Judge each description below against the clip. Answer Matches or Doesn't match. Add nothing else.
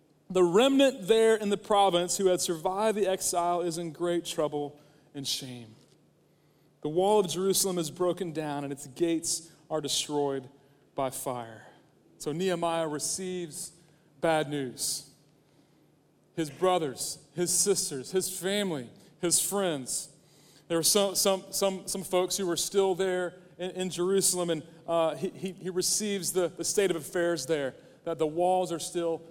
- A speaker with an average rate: Matches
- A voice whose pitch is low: Doesn't match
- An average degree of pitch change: Matches